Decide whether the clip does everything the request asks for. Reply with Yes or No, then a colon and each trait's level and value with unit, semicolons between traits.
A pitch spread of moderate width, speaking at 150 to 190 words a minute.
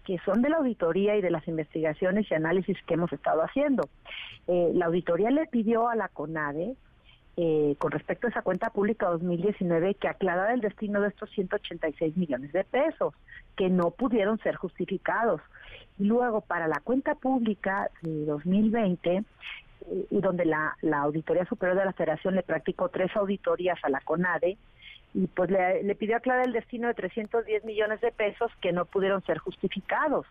Yes: average, 4.2 semitones; average, 170 wpm